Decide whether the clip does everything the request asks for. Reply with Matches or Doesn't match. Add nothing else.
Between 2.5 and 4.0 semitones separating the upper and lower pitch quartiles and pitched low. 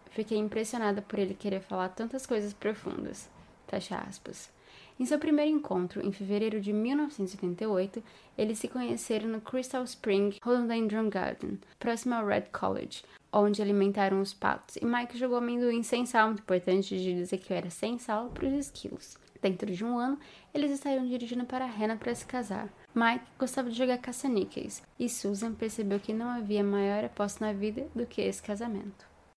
Doesn't match